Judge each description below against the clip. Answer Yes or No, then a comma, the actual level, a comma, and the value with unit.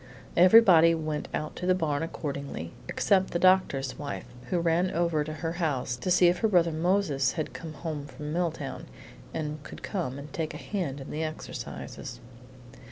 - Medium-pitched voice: Yes, medium, 160 Hz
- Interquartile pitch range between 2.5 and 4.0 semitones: Yes, average, 3.2 semitones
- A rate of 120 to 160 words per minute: No, average, 175 wpm